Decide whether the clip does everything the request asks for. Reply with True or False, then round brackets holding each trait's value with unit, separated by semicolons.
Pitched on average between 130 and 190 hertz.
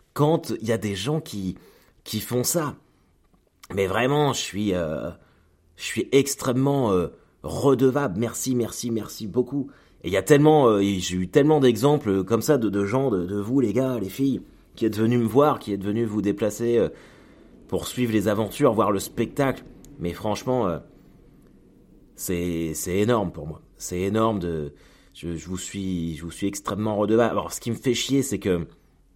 False (110 Hz)